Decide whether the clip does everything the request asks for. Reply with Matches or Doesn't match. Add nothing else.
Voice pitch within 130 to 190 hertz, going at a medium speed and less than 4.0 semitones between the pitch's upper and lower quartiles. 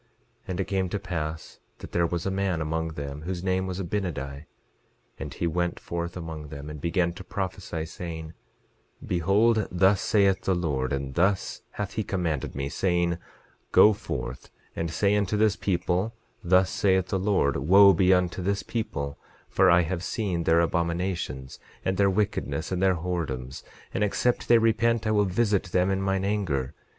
Doesn't match